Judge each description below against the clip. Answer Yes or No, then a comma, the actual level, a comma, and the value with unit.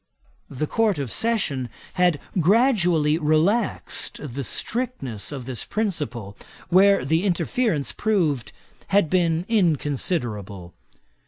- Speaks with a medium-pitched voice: Yes, medium, 160 Hz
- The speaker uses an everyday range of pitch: No, wide, 6.6 semitones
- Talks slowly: Yes, slow, 100 wpm